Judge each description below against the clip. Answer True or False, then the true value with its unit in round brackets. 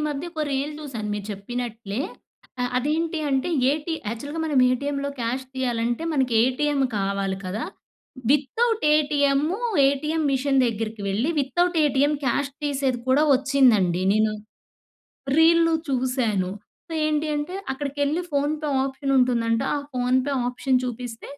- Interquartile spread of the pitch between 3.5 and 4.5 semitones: True (3.8 semitones)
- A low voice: False (270 Hz)